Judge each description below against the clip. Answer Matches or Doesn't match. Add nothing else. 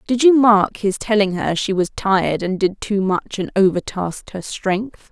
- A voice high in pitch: Matches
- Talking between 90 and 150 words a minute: Doesn't match